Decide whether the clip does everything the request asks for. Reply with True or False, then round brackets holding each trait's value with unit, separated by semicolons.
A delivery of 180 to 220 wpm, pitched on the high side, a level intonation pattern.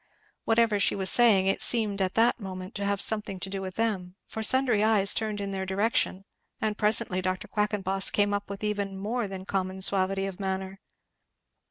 True (190 wpm; 200 Hz; 1.9 semitones)